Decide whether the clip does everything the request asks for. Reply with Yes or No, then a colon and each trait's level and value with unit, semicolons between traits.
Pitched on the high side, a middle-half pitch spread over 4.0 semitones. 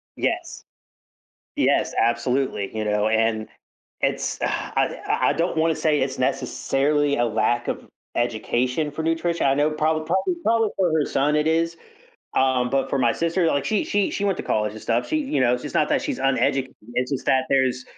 No: low, 135 Hz; average, 4.5 semitones